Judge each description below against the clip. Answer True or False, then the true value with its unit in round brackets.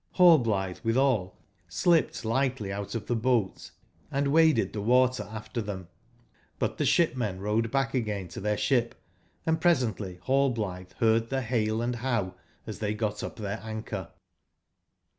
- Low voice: True (115 Hz)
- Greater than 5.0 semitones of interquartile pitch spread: False (3.8 semitones)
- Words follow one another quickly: False (150 wpm)